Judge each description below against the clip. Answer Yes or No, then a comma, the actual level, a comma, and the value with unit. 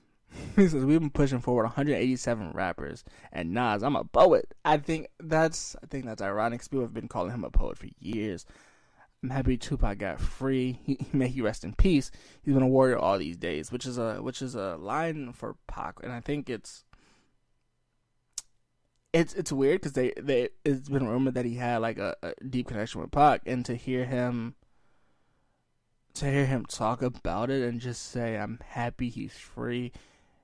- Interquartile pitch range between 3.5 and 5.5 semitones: No, narrow, 2.6 semitones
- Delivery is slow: No, average, 190 wpm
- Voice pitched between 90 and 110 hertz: No, low, 125 Hz